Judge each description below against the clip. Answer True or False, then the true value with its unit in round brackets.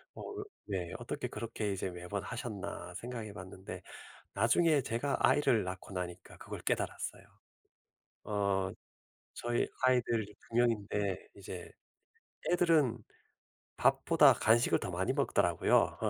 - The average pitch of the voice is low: True (110 Hz)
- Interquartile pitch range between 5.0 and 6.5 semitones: False (4.0 semitones)